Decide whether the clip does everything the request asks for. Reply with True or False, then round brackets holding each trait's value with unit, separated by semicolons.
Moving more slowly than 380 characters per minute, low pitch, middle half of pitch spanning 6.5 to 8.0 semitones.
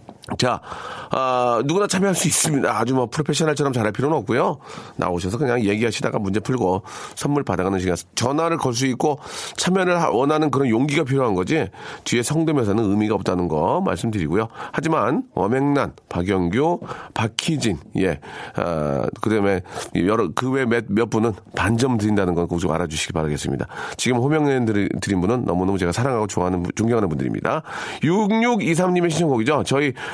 False (385 characters per minute; 120 Hz; 7.0 semitones)